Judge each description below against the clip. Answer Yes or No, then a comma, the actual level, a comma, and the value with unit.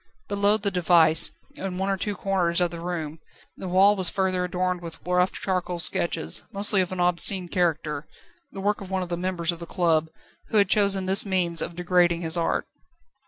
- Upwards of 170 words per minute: Yes, average, 200 wpm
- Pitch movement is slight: Yes, narrow, 2.1 semitones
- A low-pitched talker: No, medium, 180 Hz